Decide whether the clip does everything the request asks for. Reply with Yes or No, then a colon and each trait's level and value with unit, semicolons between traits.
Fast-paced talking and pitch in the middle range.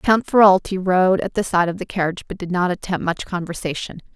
Yes: fast, 215 wpm; medium, 180 Hz